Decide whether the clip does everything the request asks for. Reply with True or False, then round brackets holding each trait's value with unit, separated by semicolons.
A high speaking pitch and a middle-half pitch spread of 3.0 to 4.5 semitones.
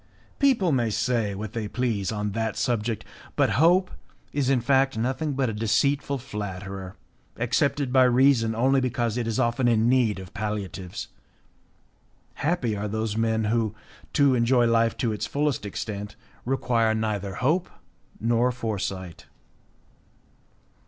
False (115 Hz; 3.6 semitones)